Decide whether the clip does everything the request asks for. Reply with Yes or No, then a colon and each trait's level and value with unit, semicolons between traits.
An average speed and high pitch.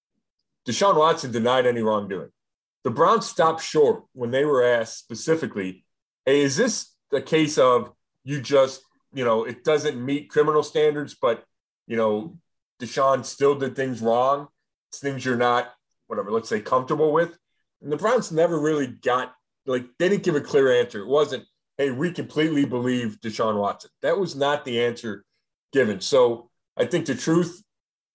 No: average, 165 wpm; low, 135 Hz